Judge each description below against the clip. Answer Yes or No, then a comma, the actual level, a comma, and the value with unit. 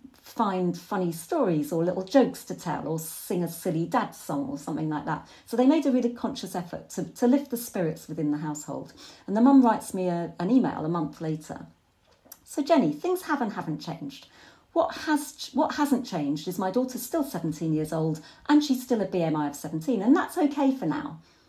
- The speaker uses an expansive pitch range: Yes, wide, 8.9 semitones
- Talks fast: Yes, fast, 210 wpm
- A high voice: Yes, high, 195 Hz